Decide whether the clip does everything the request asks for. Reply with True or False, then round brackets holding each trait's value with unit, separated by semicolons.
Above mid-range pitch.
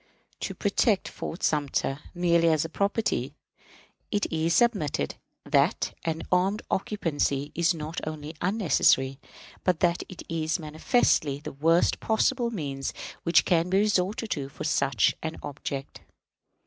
False (165 Hz)